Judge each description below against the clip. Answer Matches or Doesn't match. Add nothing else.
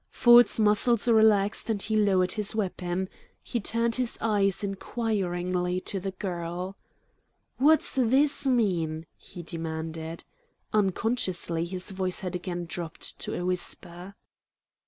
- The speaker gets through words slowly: Matches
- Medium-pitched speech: Doesn't match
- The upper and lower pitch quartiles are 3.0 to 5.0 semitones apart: Matches